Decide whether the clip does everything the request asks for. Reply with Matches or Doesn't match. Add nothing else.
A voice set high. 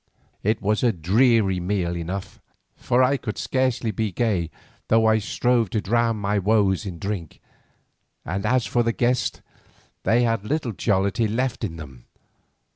Doesn't match